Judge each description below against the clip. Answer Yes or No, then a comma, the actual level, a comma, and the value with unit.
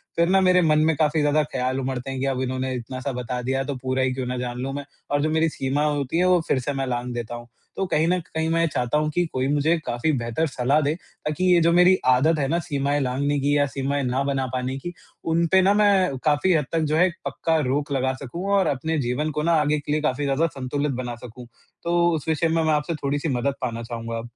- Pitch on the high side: No, medium, 145 Hz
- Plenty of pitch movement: No, average, 3.7 semitones